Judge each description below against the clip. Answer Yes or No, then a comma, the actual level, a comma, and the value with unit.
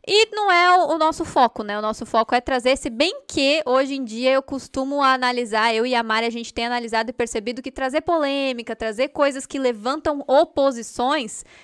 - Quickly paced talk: Yes, fast, 200 wpm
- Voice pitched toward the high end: Yes, very high, 265 Hz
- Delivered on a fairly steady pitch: No, average, 3.6 semitones